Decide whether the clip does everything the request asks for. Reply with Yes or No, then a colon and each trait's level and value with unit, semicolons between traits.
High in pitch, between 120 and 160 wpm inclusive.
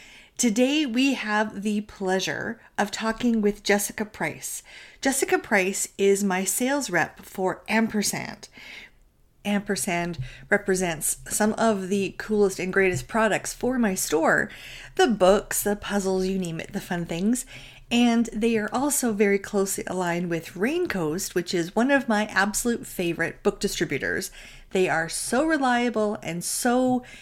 Yes: high, 205 Hz; average, 140 wpm